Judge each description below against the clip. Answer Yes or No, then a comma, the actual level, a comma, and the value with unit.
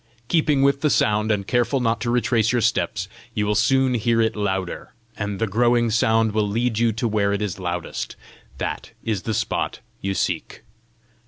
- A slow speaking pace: No, average, 185 wpm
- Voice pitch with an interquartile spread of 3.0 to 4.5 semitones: No, narrow, 2.5 semitones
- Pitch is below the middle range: Yes, low, 110 Hz